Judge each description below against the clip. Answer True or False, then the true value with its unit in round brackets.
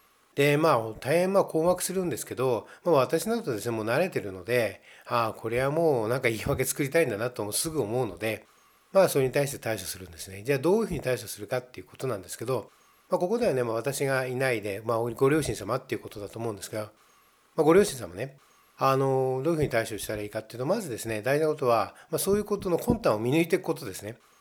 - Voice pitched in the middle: False (130 Hz)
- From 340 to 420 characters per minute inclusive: False (485 characters per minute)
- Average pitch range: False (6.2 semitones)